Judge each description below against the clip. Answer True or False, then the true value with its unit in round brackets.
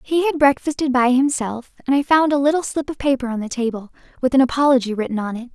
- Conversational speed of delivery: False (240 wpm)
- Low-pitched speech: False (265 Hz)